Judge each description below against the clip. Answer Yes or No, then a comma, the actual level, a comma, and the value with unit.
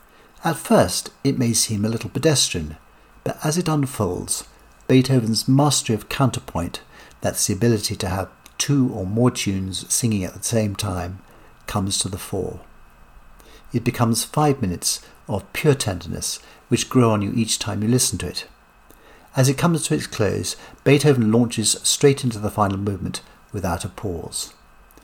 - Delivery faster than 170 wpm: No, average, 160 wpm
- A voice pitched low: Yes, low, 115 Hz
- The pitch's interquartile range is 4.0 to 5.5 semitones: Yes, average, 4.8 semitones